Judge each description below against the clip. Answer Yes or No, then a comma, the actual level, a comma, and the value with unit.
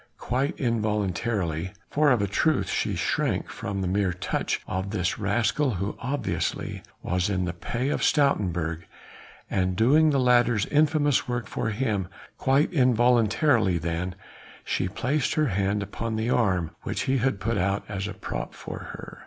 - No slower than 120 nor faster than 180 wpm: Yes, average, 160 wpm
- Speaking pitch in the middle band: No, low, 110 Hz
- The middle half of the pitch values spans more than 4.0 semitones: Yes, average, 5.2 semitones